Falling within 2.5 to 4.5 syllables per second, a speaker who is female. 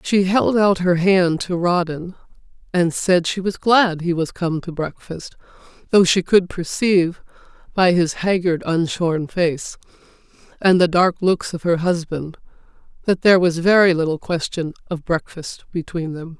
Yes: 4.4 syllables/s; female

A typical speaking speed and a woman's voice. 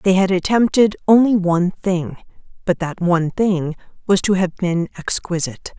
Yes: average, 155 wpm; female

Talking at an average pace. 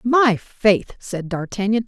No: slow, 130 wpm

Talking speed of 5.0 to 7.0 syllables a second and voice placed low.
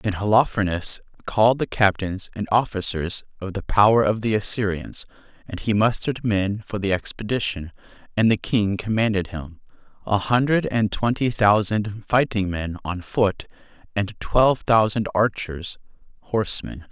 No: 4.7 syllables/s; low, 105 Hz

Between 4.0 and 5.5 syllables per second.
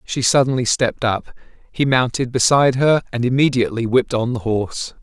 No: 5.9 syllables/s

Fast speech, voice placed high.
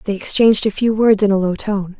Yes: fast, 270 wpm; high, 205 Hz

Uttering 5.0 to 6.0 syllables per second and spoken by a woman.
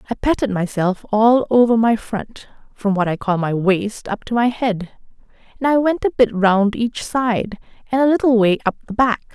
No: 4.7 syllables/s; female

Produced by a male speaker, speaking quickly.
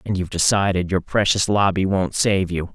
No: male; average, 195 wpm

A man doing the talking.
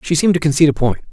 Yes: male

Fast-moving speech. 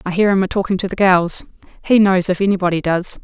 Yes: fast, 240 wpm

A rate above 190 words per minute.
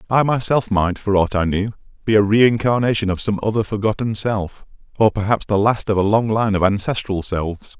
Yes: average, 200 wpm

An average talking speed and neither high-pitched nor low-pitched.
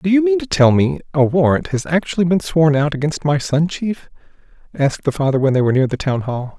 No: fast, 245 wpm; medium, 155 Hz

